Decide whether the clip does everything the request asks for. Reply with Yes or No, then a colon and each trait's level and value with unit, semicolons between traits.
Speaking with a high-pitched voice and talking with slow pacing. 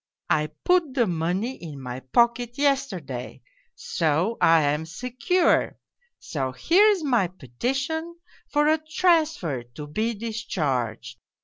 Yes: high, 220 Hz; slow, 115 wpm